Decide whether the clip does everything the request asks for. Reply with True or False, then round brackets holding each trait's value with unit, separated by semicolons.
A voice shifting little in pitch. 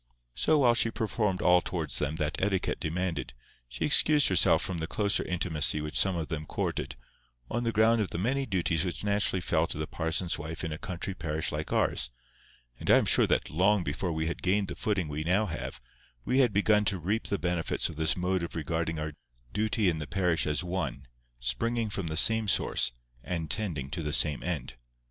False (4.5 semitones)